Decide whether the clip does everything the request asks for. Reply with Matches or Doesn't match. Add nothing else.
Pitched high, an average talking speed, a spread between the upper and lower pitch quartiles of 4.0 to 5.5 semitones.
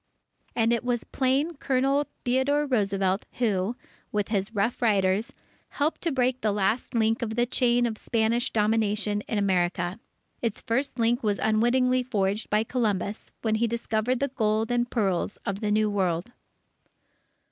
Doesn't match